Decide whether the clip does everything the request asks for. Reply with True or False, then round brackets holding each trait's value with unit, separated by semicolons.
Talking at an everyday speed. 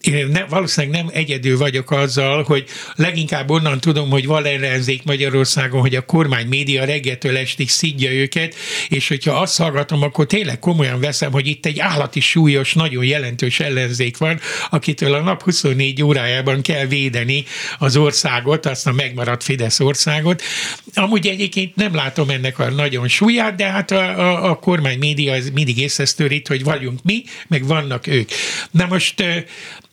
False (160 wpm)